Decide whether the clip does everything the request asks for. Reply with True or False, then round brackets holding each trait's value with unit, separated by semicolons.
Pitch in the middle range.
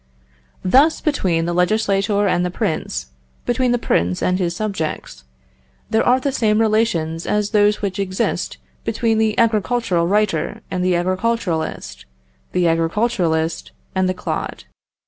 False (195 Hz)